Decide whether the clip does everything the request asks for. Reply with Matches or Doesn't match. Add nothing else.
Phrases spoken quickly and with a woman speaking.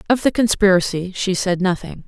Doesn't match